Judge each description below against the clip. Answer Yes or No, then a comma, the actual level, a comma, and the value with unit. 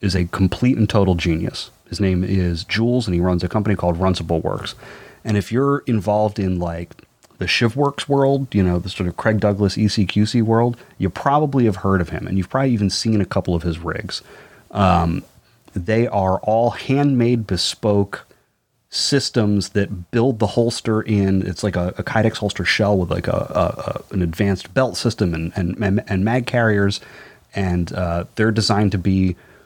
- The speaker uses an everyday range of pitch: Yes, average, 3.8 semitones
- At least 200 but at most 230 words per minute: No, average, 185 wpm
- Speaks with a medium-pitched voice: No, low, 100 Hz